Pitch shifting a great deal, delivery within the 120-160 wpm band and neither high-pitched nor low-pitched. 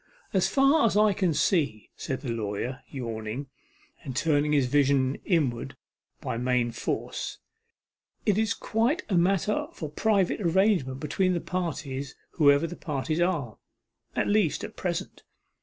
Yes: wide, 6.5 semitones; average, 140 wpm; medium, 150 Hz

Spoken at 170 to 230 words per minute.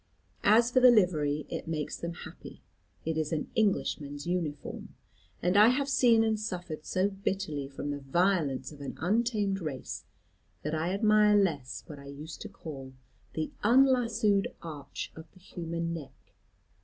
No: average, 155 wpm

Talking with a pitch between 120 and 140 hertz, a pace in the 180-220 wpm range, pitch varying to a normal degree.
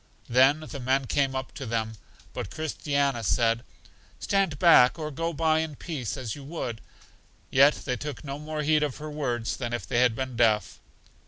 Yes: low, 135 Hz; average, 185 wpm; average, 4.1 semitones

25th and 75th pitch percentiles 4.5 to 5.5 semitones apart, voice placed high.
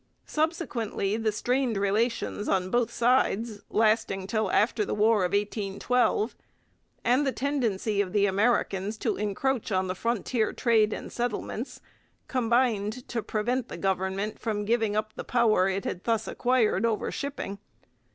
No: average, 3.1 semitones; high, 220 Hz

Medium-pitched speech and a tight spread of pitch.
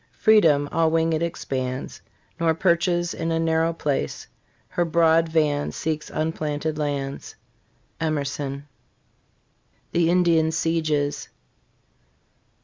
Yes: medium, 160 Hz; narrow, 2.2 semitones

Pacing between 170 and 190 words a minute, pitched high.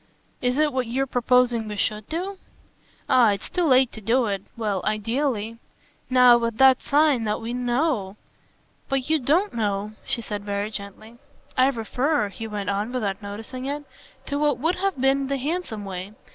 Yes: average, 180 wpm; high, 240 Hz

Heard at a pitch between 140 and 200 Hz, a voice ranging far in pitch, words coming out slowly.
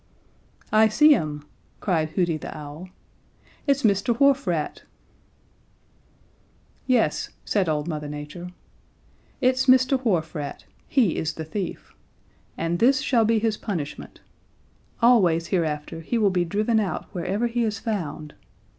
Yes: high, 190 Hz; wide, 6.4 semitones; slow, 130 wpm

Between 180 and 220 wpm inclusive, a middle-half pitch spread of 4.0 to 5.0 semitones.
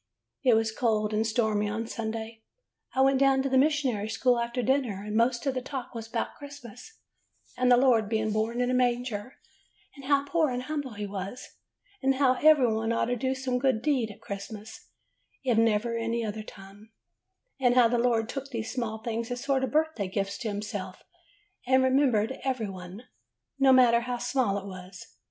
No: average, 195 wpm; average, 3.3 semitones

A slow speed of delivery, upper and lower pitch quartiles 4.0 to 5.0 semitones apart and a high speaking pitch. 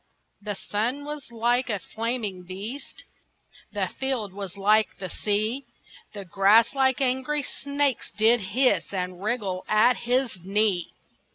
Yes: slow, 130 wpm; average, 4.4 semitones; high, 220 Hz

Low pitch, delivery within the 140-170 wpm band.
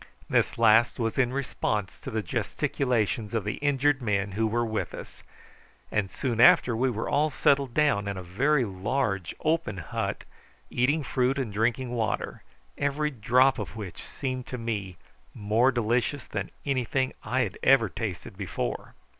Yes: low, 120 Hz; average, 160 wpm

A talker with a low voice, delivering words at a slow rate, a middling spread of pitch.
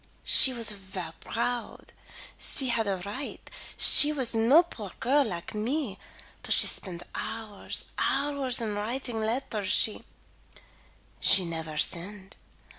No: high, 225 Hz; slow, 120 wpm; average, 5.0 semitones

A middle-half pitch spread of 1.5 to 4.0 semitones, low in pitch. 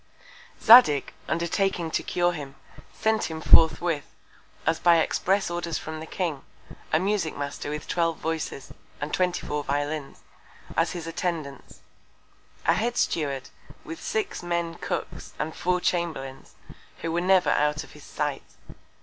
No: average, 2.8 semitones; medium, 165 Hz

